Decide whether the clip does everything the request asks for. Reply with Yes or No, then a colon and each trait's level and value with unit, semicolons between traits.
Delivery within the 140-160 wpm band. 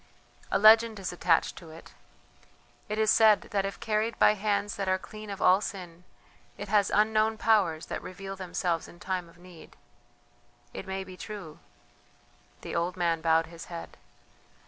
No: average, 170 wpm